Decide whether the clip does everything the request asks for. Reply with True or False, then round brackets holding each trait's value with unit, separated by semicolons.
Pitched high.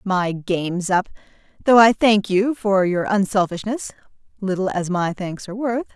True (200 Hz)